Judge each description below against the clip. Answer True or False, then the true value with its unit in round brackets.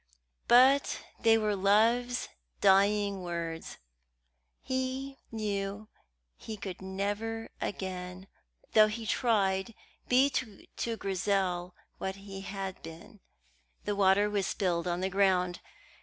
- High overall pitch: True (200 Hz)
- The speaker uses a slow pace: True (110 wpm)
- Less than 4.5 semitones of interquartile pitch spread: True (2.7 semitones)